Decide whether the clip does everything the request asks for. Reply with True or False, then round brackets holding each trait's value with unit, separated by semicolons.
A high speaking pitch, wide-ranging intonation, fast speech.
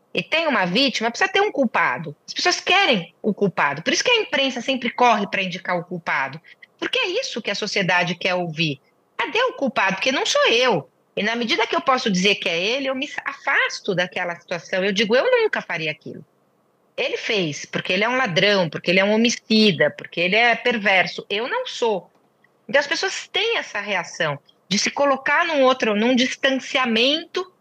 True (235 Hz; 7.4 semitones; 200 wpm)